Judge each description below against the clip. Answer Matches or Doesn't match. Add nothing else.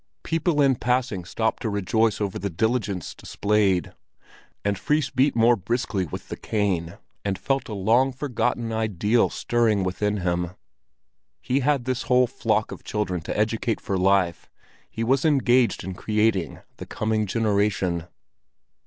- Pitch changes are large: Doesn't match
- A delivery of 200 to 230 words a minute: Doesn't match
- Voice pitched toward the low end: Matches